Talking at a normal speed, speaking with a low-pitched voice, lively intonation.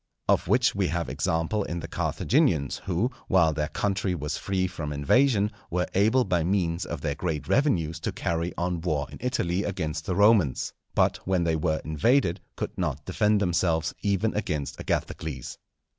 No: average, 170 wpm; very low, 85 Hz; average, 4.1 semitones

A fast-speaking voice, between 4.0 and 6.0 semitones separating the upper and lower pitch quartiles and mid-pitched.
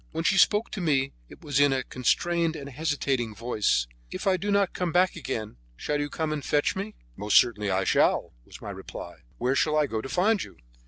Yes: fast, 220 wpm; wide, 5.6 semitones; medium, 145 Hz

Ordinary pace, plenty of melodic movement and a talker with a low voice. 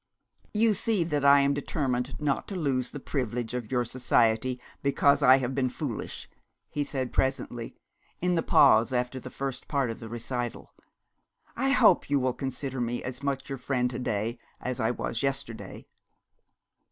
No: average, 170 wpm; narrow, 2.5 semitones; low, 130 Hz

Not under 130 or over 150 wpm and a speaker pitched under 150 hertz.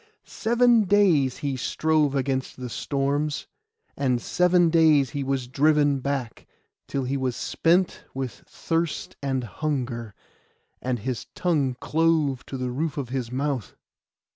Yes: slow, 135 wpm; medium, 140 Hz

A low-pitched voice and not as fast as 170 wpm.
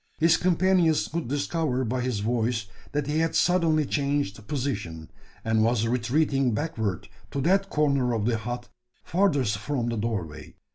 Yes: low, 130 Hz; average, 150 wpm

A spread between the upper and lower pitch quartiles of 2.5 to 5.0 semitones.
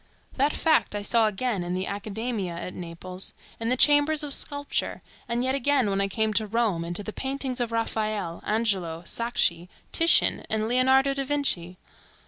No: wide, 5.6 semitones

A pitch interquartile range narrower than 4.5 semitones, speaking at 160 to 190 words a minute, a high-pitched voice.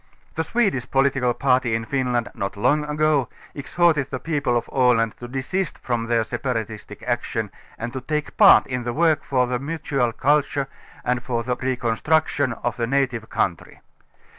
No: average, 3.0 semitones; average, 165 wpm; low, 125 Hz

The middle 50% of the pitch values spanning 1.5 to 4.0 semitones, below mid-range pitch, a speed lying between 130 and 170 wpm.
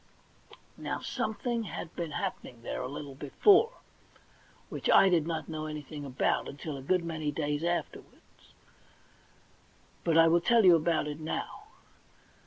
No: average, 2.8 semitones; medium, 160 Hz; average, 145 wpm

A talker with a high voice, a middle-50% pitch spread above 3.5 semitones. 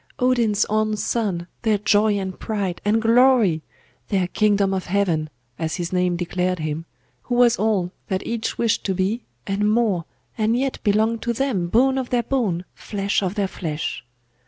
Yes: high, 205 Hz; average, 3.9 semitones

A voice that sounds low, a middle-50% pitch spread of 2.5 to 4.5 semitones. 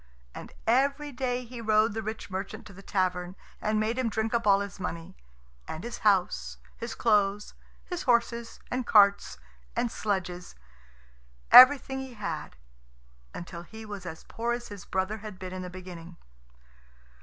No: high, 210 Hz; average, 4.1 semitones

